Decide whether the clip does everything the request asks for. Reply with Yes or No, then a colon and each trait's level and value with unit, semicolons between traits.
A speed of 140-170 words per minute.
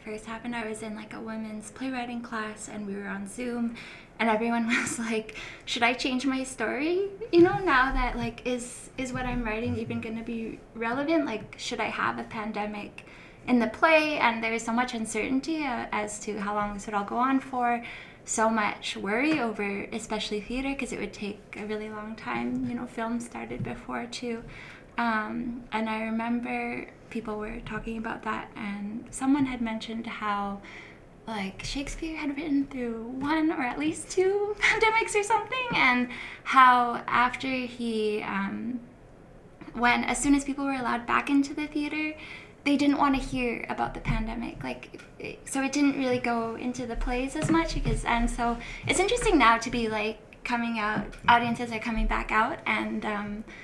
No: average, 185 wpm